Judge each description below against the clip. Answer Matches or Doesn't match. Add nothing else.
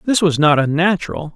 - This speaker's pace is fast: Doesn't match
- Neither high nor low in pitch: Matches